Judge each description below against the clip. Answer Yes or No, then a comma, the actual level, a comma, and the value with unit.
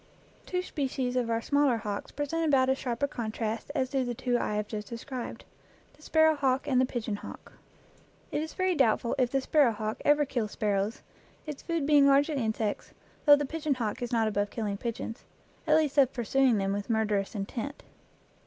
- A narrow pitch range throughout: No, average, 4.6 semitones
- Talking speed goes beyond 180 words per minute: Yes, average, 200 wpm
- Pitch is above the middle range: Yes, very high, 250 Hz